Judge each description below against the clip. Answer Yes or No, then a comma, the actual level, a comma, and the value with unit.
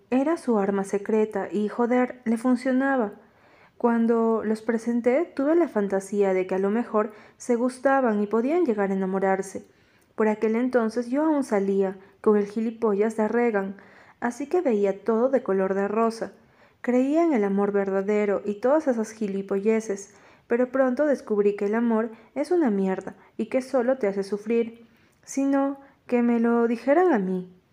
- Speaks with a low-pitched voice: No, high, 225 Hz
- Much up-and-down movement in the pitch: No, average, 3.7 semitones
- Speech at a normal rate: Yes, average, 165 wpm